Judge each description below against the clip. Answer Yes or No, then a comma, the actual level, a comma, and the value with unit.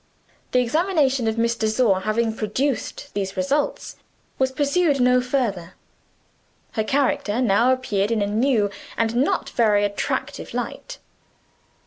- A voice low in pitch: No, high, 235 Hz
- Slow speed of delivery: Yes, slow, 130 wpm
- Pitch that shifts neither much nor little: Yes, average, 4.0 semitones